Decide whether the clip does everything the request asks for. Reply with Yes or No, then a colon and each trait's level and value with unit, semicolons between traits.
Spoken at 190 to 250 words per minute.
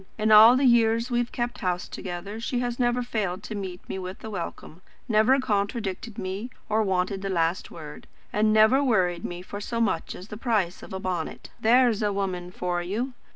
Yes: average, 200 wpm